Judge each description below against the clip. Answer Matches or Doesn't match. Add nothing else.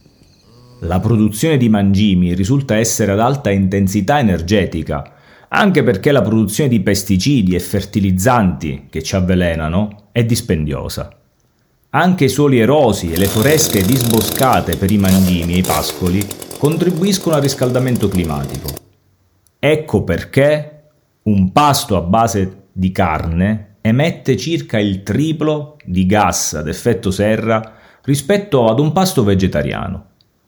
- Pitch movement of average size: Doesn't match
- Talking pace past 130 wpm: Doesn't match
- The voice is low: Matches